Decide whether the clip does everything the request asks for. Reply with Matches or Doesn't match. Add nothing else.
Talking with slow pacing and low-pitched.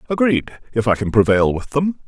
Doesn't match